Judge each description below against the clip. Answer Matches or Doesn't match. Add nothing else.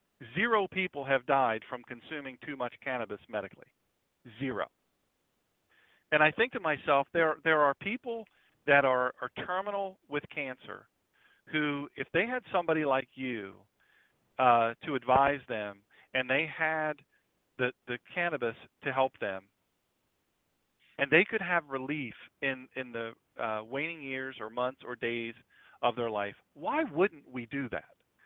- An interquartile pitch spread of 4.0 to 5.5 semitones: Matches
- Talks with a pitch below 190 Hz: Matches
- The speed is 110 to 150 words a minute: Matches